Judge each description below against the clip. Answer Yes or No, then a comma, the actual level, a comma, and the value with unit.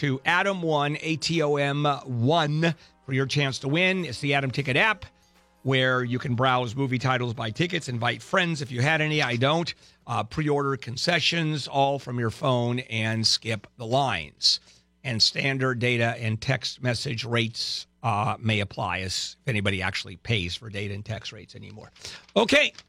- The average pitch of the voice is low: Yes, low, 130 Hz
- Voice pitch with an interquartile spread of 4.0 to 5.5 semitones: Yes, average, 4.3 semitones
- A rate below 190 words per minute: Yes, average, 180 wpm